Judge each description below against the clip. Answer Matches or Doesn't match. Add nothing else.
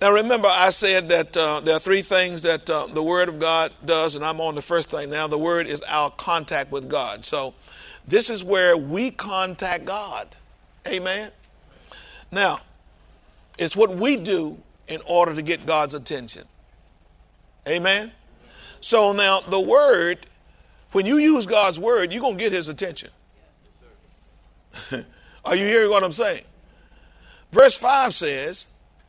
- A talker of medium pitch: Matches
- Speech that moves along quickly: Doesn't match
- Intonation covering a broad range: Doesn't match